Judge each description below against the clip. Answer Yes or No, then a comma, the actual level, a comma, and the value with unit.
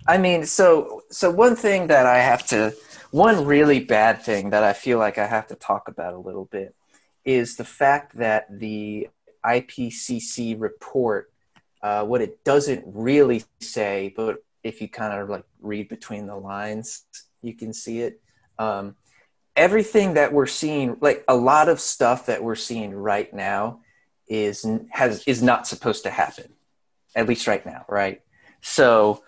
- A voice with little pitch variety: No, average, 4.6 semitones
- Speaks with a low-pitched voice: Yes, low, 115 Hz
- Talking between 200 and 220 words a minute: No, average, 165 wpm